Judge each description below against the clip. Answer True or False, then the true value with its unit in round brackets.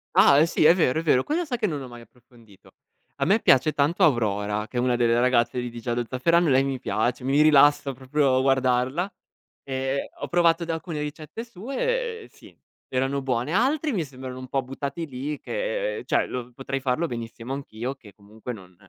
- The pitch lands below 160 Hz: True (135 Hz)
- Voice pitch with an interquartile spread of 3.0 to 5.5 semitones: True (5.0 semitones)